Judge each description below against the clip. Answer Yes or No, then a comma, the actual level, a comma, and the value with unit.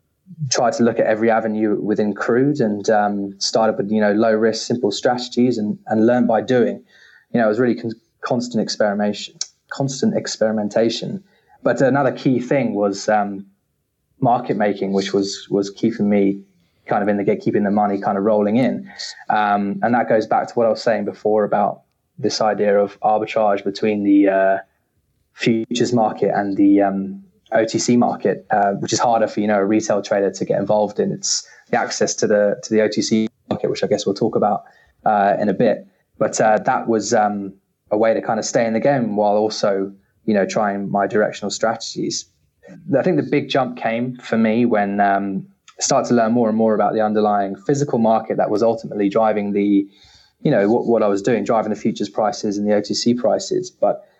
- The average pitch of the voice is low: Yes, low, 105 Hz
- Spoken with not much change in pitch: Yes, narrow, 2.0 semitones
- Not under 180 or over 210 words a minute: Yes, average, 200 wpm